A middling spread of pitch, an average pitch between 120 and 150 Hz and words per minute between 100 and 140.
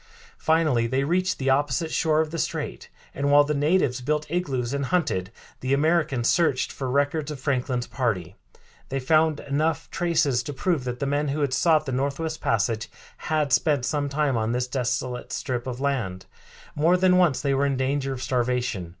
No: average, 3.4 semitones; medium, 140 Hz; average, 185 wpm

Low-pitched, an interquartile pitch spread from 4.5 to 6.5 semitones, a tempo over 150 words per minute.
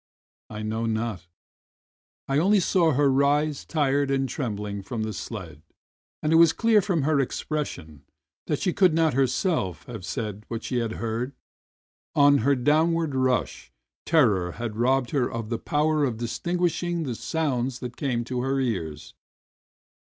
Yes: low, 130 Hz; average, 5.2 semitones; average, 160 wpm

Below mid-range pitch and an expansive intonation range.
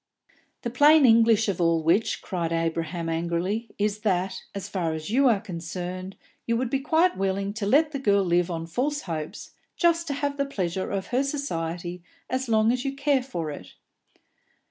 No: high, 200 Hz; wide, 7.1 semitones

